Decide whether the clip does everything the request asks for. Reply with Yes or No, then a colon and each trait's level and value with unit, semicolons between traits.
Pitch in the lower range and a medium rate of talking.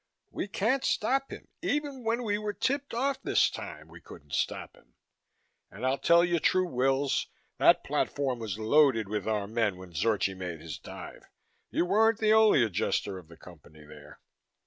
Yes: low, 130 Hz; average, 175 wpm